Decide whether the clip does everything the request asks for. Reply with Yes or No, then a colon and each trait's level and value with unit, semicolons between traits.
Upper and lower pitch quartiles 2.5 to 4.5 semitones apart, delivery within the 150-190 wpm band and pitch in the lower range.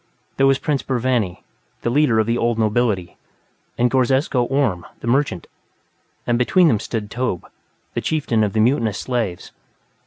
Yes: average, 3.4 semitones; average, 155 wpm; low, 120 Hz